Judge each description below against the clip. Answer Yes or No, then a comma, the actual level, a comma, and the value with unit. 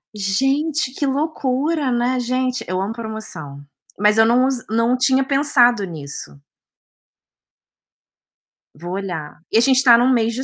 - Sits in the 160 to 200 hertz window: No, high, 240 Hz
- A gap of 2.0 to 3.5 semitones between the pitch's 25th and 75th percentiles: No, average, 4.5 semitones